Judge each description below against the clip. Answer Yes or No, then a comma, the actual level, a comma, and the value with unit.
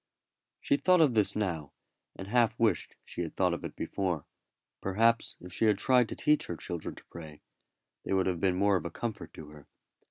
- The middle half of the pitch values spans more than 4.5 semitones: Yes, average, 5.1 semitones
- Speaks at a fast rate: Yes, fast, 210 wpm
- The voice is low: Yes, very low, 95 Hz